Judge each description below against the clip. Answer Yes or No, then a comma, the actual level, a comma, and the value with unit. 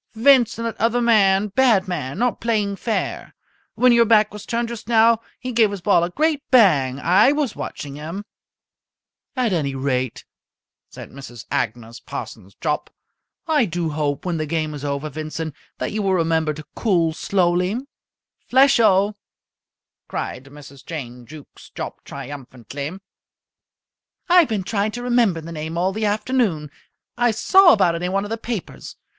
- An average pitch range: No, wide, 7.0 semitones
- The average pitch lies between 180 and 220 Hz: Yes, high, 190 Hz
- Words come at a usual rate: Yes, average, 160 wpm